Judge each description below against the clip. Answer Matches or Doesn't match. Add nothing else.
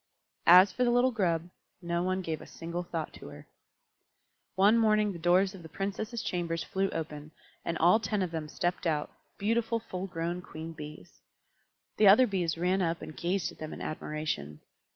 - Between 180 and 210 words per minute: Matches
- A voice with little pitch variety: Doesn't match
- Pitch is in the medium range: Matches